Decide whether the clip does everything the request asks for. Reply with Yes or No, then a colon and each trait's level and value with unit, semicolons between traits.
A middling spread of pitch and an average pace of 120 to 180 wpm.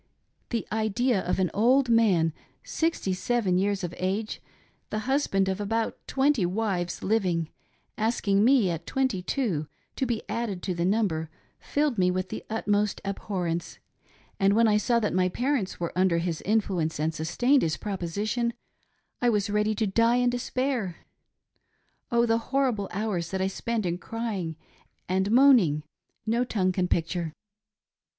Yes: average, 4.3 semitones; average, 155 wpm